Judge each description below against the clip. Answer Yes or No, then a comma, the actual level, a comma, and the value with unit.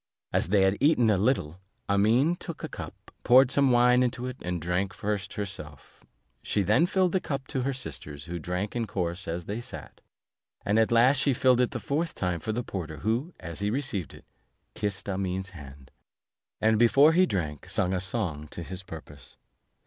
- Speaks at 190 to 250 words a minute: Yes, average, 195 wpm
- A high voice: No, low, 105 Hz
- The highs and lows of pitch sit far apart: Yes, wide, 6.0 semitones